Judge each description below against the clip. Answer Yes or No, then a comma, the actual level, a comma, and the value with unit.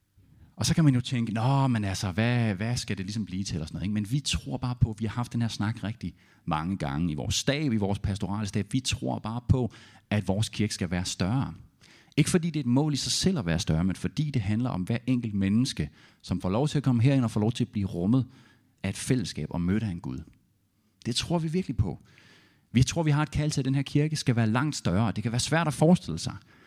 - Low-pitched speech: Yes, low, 110 Hz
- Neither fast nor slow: No, fast, 270 wpm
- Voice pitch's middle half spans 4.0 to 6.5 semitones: Yes, average, 4.7 semitones